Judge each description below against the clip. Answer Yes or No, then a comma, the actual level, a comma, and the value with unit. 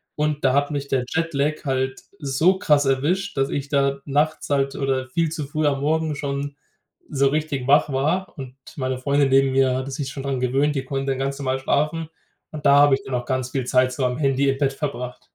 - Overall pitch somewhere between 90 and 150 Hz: Yes, medium, 140 Hz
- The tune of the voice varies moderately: No, narrow, 1.8 semitones